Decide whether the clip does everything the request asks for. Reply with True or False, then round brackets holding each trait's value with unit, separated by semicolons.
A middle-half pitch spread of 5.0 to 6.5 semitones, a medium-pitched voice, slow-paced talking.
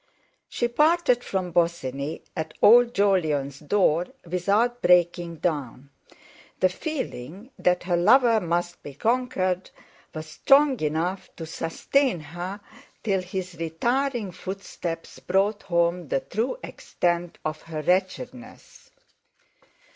True (5.3 semitones; 180 Hz; 110 wpm)